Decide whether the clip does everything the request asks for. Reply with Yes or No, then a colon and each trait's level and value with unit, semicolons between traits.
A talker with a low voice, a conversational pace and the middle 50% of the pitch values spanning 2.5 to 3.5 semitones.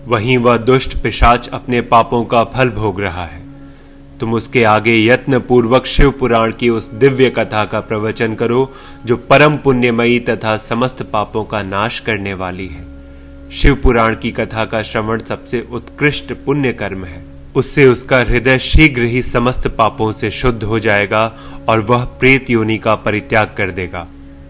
Yes: low, 115 Hz; average, 160 wpm; average, 2.9 semitones